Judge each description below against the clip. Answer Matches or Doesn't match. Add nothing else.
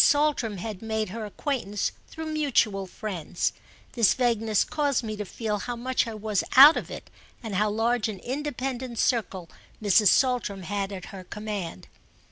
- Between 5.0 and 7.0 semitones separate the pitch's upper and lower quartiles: Doesn't match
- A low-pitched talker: Doesn't match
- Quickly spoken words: Doesn't match